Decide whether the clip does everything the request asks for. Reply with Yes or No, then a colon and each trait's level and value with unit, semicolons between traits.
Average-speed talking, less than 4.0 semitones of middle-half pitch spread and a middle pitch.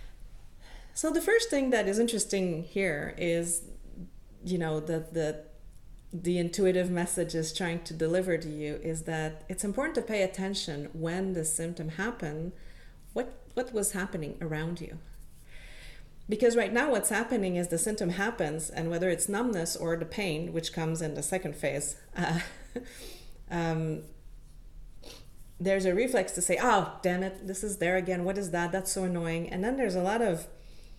Yes: average, 170 wpm; average, 3.3 semitones; medium, 175 Hz